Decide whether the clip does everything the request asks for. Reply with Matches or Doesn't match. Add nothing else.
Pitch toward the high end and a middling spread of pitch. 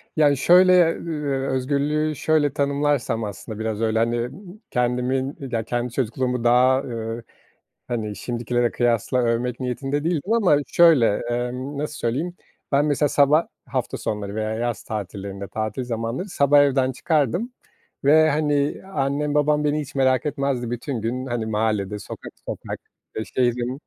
Doesn't match